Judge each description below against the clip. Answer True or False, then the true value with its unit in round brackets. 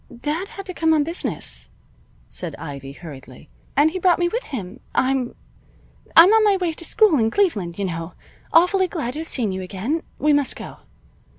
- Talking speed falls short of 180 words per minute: False (190 wpm)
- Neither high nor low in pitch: False (290 Hz)